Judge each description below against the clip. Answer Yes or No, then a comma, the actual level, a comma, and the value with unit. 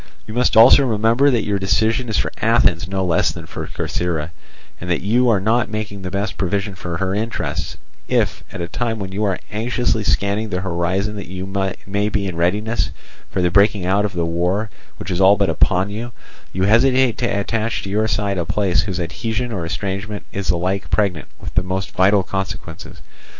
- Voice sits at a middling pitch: No, low, 100 Hz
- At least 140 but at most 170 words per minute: No, average, 195 wpm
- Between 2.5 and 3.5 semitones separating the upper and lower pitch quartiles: Yes, average, 2.9 semitones